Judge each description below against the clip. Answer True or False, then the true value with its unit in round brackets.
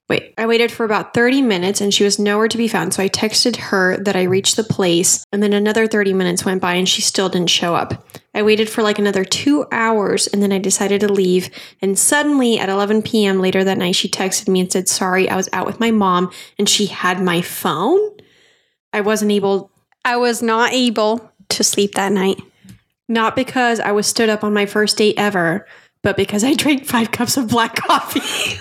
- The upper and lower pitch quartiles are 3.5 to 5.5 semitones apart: False (3.0 semitones)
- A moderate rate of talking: False (220 wpm)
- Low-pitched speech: False (205 Hz)